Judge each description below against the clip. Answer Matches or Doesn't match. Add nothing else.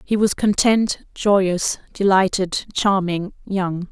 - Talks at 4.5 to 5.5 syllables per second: Doesn't match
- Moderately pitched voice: Doesn't match